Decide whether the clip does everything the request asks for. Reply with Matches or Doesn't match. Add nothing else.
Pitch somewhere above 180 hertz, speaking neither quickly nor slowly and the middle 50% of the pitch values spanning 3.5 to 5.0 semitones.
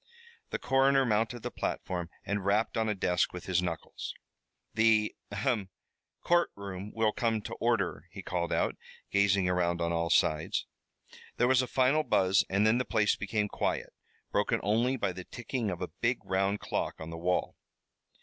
Doesn't match